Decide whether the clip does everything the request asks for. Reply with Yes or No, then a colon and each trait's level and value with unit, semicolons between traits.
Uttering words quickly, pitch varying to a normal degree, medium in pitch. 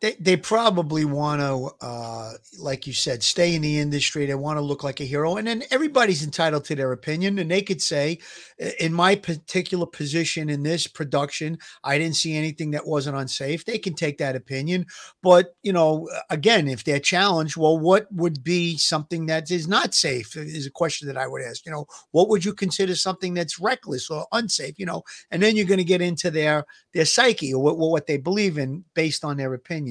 Yes: fast, 215 wpm; average, 3.8 semitones; medium, 160 Hz